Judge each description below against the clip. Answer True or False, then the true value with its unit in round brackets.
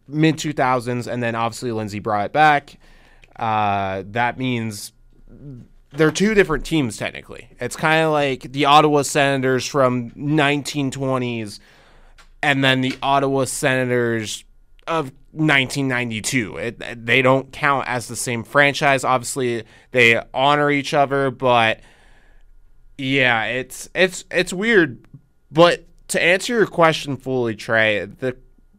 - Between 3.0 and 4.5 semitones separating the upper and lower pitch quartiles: True (3.7 semitones)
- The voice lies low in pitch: True (130 Hz)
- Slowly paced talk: True (130 wpm)